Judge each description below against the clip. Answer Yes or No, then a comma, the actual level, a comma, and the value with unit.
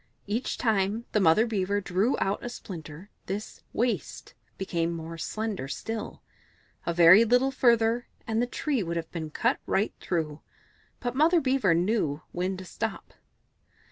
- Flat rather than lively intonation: No, average, 5.3 semitones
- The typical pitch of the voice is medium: No, high, 205 Hz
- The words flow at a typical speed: Yes, average, 150 wpm